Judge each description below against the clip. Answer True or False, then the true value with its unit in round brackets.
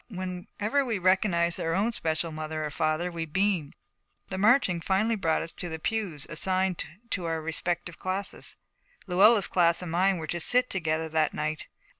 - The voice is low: False (175 Hz)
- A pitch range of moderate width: True (3.2 semitones)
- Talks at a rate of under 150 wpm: False (170 wpm)